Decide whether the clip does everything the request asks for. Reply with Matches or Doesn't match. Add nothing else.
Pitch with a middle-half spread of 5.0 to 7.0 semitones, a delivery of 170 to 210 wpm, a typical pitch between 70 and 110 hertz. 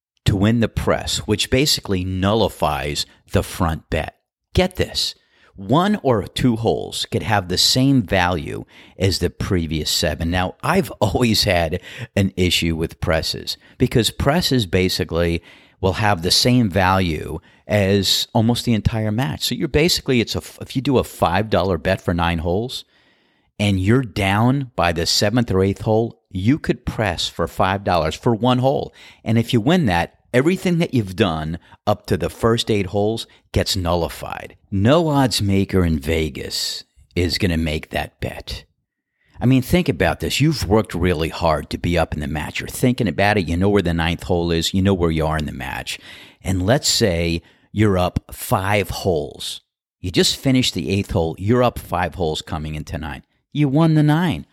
Matches